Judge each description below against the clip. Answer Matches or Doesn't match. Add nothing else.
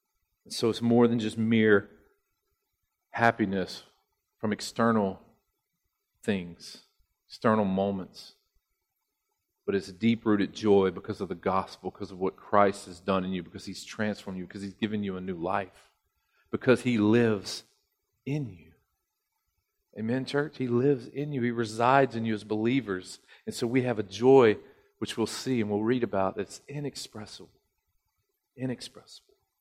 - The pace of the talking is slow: Doesn't match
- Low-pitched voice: Matches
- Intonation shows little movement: Doesn't match